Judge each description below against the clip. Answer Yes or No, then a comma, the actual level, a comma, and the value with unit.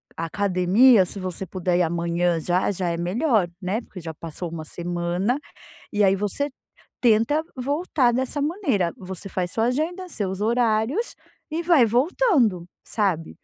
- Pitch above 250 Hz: No, high, 205 Hz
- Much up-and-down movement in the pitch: Yes, wide, 6.2 semitones